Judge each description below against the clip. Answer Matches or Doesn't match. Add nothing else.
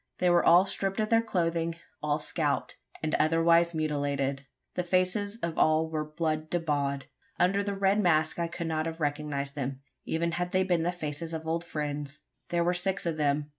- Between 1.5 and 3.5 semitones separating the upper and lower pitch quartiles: Matches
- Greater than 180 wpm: Matches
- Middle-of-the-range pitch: Matches